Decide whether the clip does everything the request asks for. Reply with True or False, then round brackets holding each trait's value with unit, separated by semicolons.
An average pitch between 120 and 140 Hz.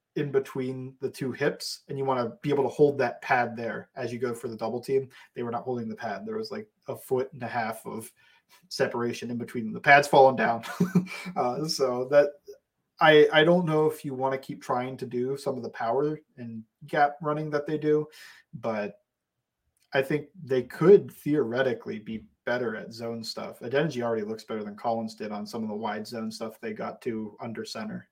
True (135 Hz)